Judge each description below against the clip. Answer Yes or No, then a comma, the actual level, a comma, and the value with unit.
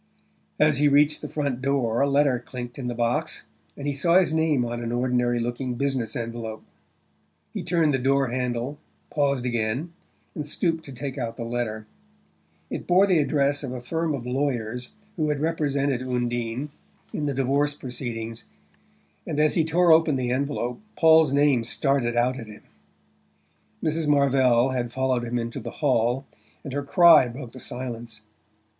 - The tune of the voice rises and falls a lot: No, average, 3.3 semitones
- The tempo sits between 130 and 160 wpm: No, average, 170 wpm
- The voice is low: Yes, low, 130 Hz